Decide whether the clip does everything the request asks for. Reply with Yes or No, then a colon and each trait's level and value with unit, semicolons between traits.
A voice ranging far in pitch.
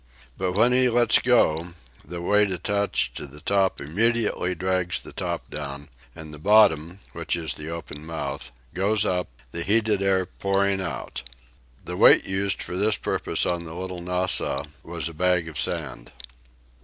No: average, 3.5 semitones